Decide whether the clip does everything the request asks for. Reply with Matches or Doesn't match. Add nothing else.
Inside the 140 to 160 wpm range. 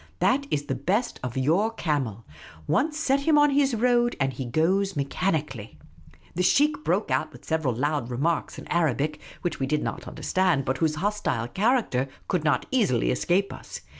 Doesn't match